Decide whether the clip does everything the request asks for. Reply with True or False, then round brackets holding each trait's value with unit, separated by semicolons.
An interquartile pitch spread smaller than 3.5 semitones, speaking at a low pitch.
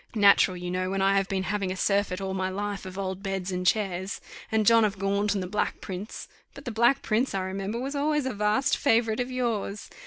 False (2.9 semitones; 200 Hz)